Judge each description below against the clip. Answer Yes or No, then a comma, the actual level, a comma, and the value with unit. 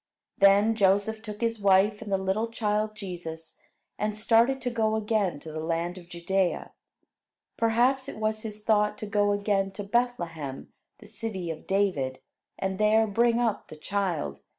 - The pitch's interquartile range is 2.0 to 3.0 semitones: Yes, average, 2.7 semitones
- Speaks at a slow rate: No, average, 165 wpm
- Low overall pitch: No, high, 205 Hz